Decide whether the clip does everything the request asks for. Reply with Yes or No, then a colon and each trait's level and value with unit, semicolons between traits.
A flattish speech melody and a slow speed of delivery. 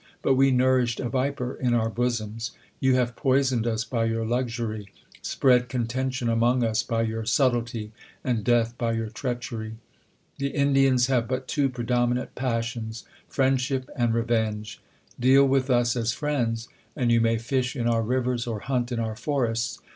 No: narrow, 2.1 semitones; average, 165 wpm